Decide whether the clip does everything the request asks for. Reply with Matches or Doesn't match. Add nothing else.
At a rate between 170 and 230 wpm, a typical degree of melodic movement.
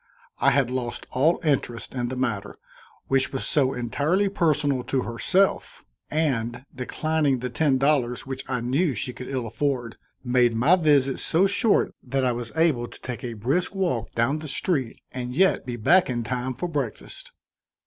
Matches